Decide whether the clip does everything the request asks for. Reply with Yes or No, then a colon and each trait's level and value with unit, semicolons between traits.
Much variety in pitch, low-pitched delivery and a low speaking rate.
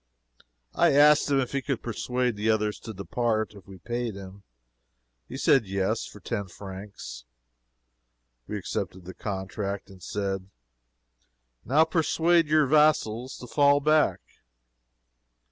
Yes: wide, 6.1 semitones; low, 110 Hz; slow, 130 wpm